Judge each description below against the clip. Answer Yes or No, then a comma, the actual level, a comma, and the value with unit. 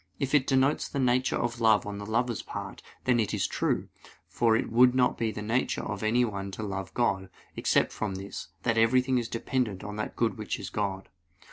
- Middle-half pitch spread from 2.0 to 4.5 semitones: Yes, average, 3.2 semitones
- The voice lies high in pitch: No, low, 115 Hz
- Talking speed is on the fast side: Yes, fast, 215 wpm